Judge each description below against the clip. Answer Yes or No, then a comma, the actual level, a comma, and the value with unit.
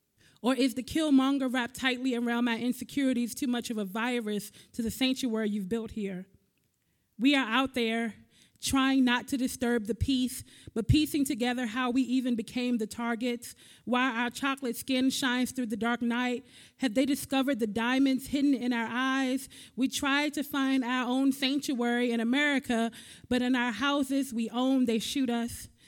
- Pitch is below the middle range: No, very high, 250 Hz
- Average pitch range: No, narrow, 2.0 semitones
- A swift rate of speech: No, average, 175 wpm